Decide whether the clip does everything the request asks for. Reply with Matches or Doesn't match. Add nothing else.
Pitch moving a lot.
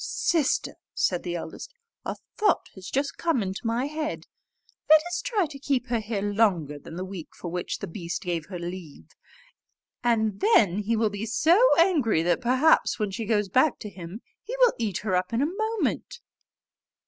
Matches